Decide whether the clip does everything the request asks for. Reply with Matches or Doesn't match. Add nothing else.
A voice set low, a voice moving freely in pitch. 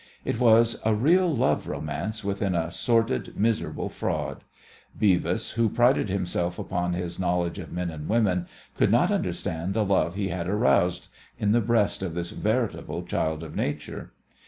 Doesn't match